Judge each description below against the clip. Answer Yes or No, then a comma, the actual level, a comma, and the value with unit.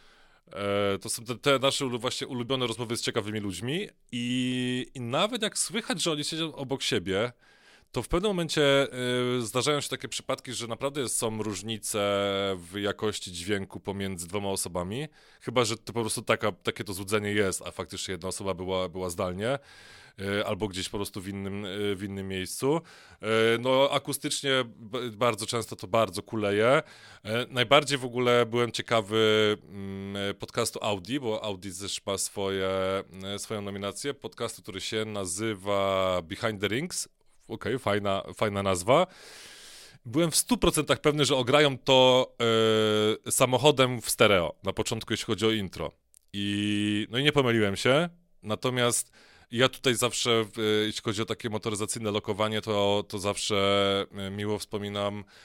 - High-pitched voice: No, low, 110 Hz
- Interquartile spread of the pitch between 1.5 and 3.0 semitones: No, average, 3.8 semitones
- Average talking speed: Yes, average, 150 wpm